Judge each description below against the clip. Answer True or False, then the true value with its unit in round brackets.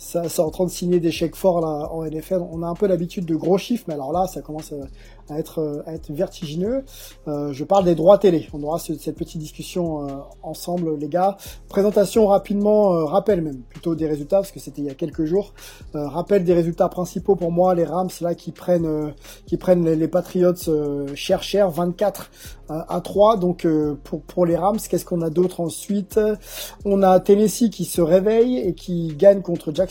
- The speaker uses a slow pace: False (215 wpm)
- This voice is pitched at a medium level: True (175 Hz)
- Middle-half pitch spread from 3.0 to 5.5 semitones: True (3.4 semitones)